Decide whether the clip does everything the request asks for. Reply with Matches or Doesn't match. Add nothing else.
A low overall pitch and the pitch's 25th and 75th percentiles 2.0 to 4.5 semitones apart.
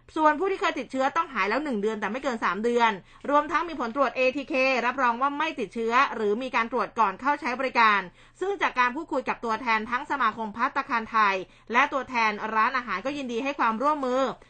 Doesn't match